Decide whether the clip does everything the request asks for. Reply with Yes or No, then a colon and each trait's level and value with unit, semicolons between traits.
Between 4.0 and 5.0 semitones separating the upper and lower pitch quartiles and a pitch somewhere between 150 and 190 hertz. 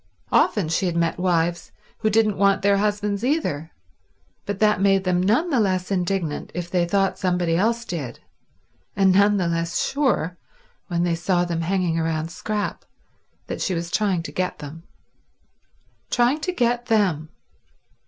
No: average, 3.5 semitones; medium, 185 Hz